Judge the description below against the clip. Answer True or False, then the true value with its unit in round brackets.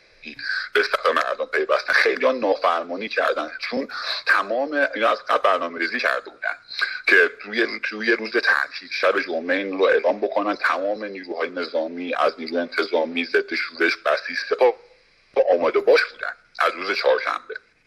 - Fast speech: False (140 wpm)